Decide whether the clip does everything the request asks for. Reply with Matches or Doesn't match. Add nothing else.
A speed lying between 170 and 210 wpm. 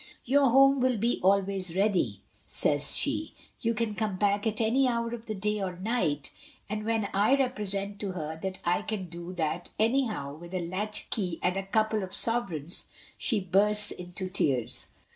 Matches